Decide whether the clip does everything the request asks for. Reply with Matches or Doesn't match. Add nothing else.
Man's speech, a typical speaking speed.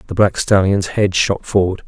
Matches